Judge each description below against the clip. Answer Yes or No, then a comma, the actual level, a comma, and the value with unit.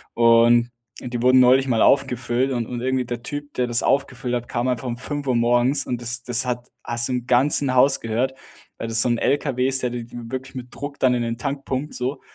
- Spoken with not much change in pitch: Yes, narrow, 1.8 semitones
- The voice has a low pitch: Yes, low, 125 Hz